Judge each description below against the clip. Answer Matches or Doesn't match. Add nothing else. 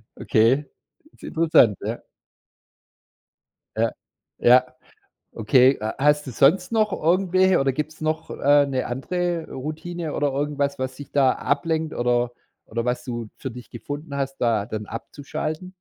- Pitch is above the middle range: Doesn't match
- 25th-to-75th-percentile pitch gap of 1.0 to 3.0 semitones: Doesn't match